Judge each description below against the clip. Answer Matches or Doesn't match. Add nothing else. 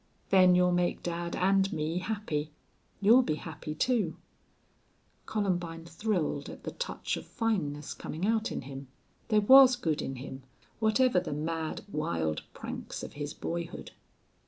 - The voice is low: Doesn't match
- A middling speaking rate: Matches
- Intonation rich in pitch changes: Matches